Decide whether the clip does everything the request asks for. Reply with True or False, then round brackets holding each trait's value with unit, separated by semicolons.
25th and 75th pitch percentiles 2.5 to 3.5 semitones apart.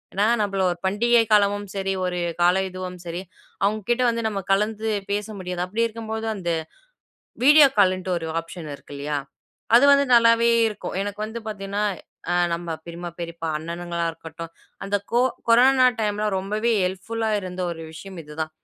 False (4.0 semitones)